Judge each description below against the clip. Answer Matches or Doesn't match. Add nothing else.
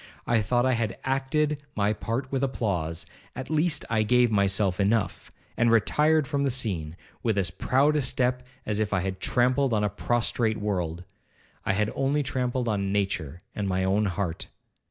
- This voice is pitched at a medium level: Doesn't match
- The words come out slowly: Doesn't match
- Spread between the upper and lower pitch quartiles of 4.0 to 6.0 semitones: Matches